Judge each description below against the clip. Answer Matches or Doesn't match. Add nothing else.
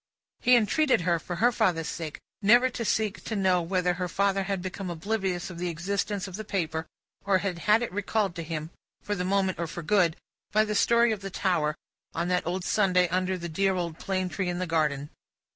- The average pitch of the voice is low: Doesn't match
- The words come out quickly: Matches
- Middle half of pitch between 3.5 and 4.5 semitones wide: Doesn't match